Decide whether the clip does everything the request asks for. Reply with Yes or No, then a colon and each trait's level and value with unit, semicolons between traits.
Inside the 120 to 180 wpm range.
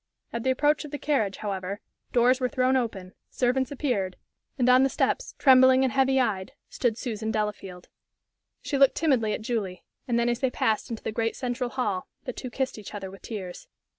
No: average, 195 wpm